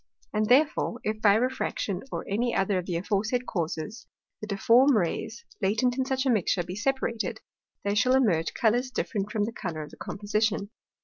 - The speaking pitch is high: Yes, high, 215 Hz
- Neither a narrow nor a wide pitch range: Yes, average, 3.9 semitones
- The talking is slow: No, average, 180 wpm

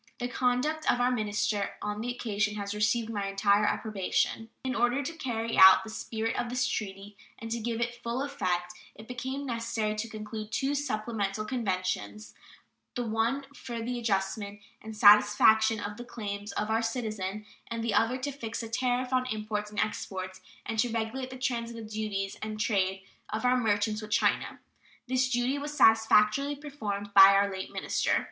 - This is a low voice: No, high, 220 Hz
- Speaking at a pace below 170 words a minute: No, average, 175 wpm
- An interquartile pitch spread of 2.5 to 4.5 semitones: Yes, average, 2.8 semitones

